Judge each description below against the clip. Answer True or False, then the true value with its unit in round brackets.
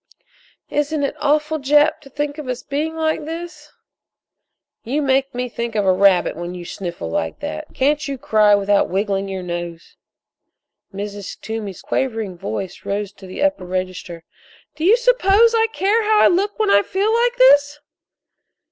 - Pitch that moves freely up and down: True (8.2 semitones)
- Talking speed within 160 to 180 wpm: True (165 wpm)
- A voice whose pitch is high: True (265 Hz)